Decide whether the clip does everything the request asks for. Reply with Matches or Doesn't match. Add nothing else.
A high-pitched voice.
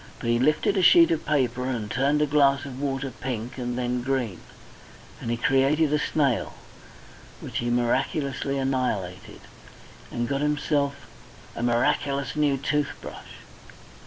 Doesn't match